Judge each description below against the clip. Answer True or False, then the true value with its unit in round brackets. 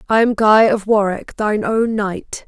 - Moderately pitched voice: False (210 Hz)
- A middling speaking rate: True (195 wpm)